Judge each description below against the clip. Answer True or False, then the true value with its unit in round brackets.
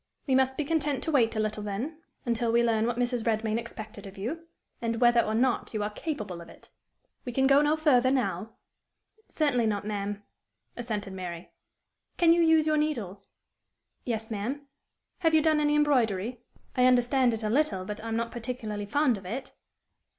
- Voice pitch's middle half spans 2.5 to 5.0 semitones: True (4.7 semitones)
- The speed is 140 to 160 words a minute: False (185 wpm)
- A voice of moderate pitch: False (240 Hz)